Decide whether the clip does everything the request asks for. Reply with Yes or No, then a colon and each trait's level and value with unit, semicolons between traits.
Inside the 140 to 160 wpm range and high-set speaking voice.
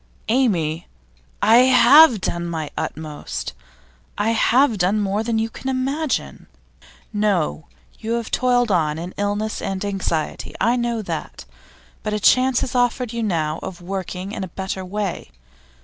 Yes: average, 150 wpm; high, 210 Hz